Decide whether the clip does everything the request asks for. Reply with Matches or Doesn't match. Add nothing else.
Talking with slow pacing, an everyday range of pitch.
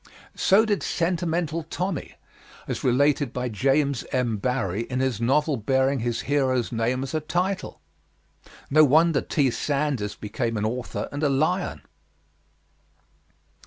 Matches